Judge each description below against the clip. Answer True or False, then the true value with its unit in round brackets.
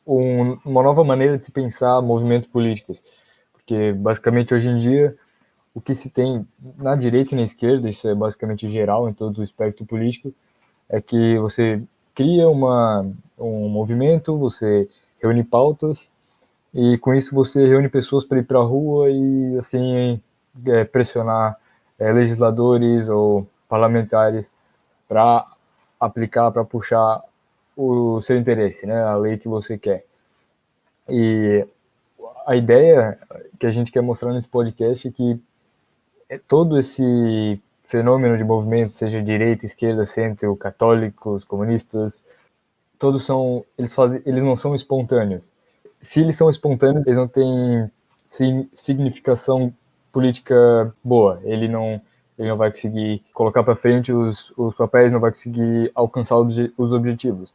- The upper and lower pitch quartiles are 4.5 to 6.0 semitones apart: False (2.7 semitones)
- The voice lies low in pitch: True (120 Hz)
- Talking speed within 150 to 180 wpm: False (140 wpm)